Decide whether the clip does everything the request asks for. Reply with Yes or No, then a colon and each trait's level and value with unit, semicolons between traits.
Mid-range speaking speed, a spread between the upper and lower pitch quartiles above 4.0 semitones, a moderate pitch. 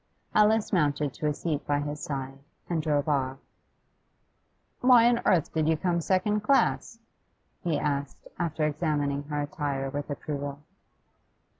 No: average, 145 wpm; average, 3.2 semitones; medium, 150 Hz